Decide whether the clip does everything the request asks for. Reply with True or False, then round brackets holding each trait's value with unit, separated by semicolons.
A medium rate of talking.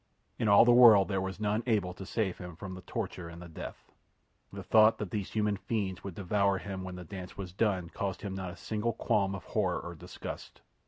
False (225 wpm)